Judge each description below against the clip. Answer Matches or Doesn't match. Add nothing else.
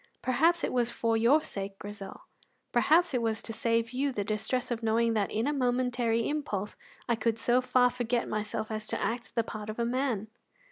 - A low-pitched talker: Doesn't match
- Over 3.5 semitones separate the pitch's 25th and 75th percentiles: Doesn't match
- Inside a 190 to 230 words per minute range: Matches